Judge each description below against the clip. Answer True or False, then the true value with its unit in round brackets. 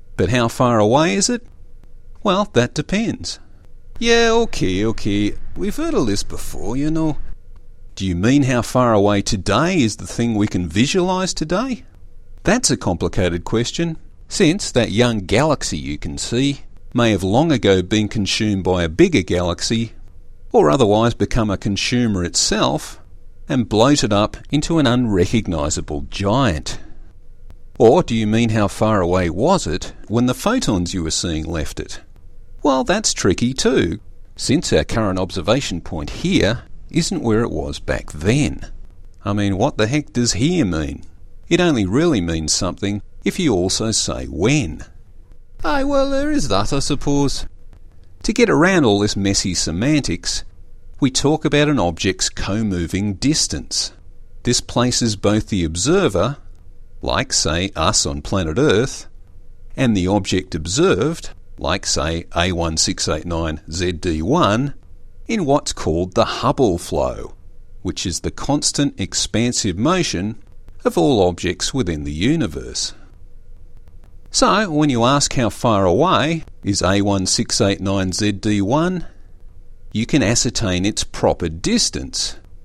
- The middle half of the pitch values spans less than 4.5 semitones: False (5.2 semitones)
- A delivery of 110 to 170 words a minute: True (140 wpm)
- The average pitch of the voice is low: True (100 Hz)